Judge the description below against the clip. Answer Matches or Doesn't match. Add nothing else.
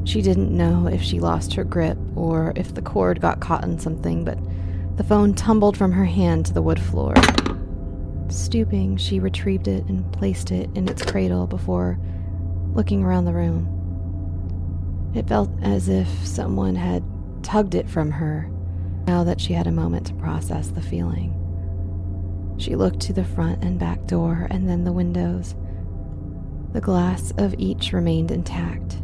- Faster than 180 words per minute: Doesn't match